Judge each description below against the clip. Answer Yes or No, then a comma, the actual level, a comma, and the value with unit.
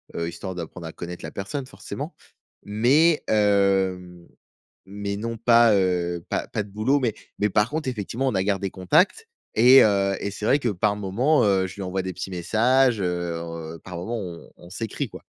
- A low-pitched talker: Yes, low, 100 Hz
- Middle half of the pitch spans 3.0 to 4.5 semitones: Yes, average, 4.2 semitones